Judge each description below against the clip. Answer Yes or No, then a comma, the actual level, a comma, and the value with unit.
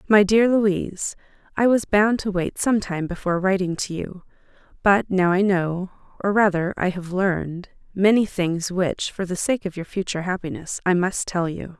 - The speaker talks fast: No, average, 185 wpm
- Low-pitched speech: No, high, 190 Hz